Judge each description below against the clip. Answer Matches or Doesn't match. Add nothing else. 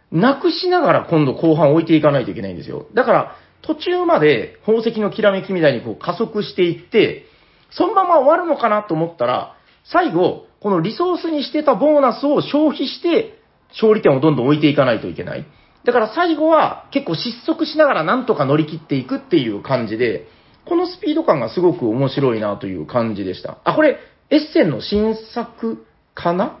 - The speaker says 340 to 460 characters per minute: Matches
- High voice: Matches